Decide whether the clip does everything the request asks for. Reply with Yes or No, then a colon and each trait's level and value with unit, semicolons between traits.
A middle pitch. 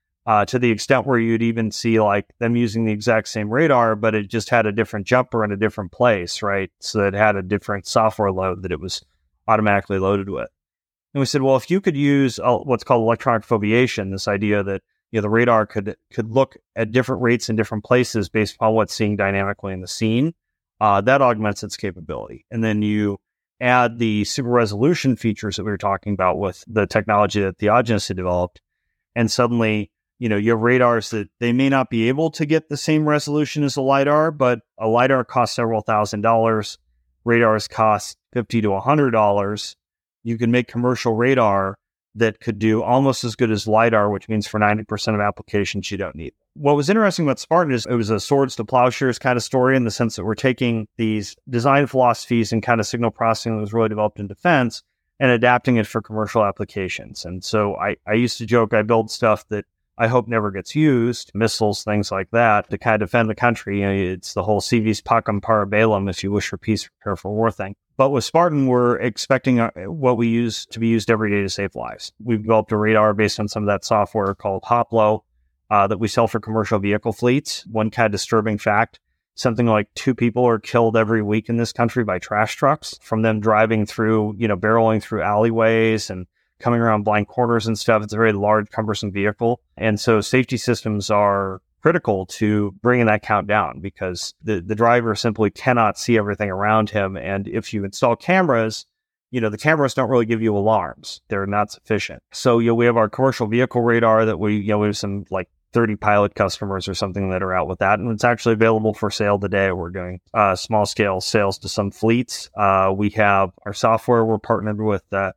No: low, 110 Hz